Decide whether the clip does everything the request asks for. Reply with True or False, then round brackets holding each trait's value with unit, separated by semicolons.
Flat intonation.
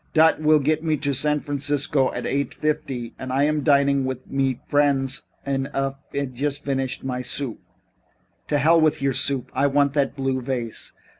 True (1.7 semitones)